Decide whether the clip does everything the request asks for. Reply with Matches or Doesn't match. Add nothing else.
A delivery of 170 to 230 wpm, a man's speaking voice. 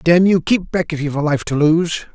Doesn't match